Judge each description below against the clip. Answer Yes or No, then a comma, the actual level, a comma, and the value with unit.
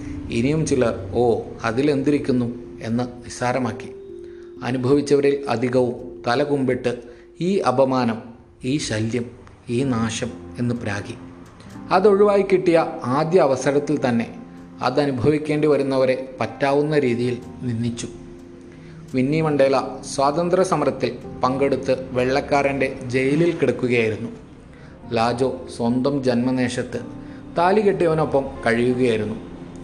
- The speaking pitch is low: Yes, low, 130 Hz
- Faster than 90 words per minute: No, average, 80 wpm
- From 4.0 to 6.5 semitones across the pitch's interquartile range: No, average, 3.2 semitones